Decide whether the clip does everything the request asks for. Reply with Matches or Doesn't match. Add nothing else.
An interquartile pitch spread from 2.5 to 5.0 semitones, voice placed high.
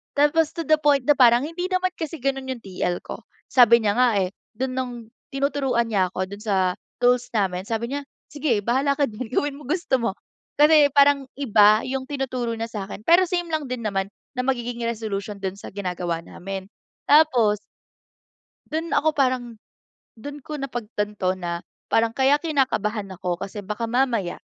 Doesn't match